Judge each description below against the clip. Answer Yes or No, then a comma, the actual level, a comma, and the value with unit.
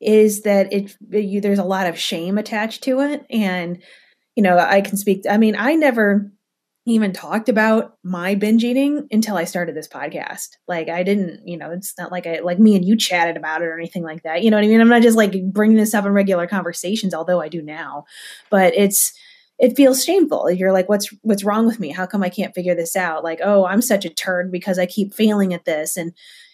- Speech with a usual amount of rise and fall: Yes, average, 3.5 semitones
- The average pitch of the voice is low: No, high, 200 Hz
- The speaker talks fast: Yes, fast, 235 wpm